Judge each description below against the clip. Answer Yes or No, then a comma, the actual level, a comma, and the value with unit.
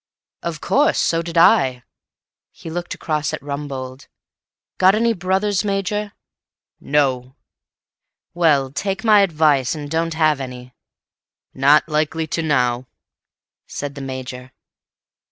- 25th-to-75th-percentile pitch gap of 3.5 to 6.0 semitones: Yes, average, 4.7 semitones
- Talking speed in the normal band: No, slow, 120 wpm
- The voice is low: No, medium, 155 Hz